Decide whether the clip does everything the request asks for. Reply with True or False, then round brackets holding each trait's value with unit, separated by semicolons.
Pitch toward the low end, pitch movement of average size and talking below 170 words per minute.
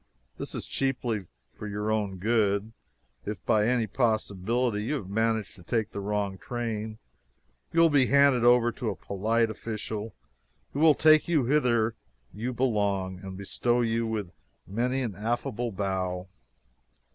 True (110 Hz; 3.1 semitones; 150 wpm)